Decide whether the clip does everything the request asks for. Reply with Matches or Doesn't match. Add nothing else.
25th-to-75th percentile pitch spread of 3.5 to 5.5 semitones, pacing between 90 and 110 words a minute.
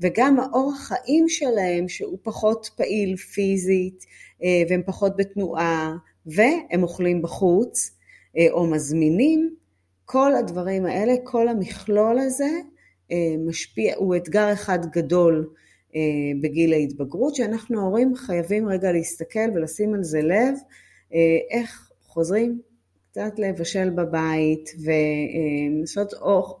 Matches